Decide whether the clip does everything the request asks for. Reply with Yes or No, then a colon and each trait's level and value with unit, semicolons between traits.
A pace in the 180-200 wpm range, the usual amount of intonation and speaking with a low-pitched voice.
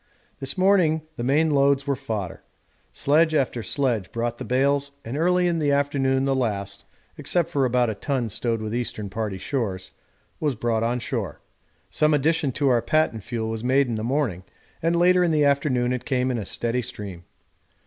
Yes: average, 190 wpm; average, 4.2 semitones; low, 130 Hz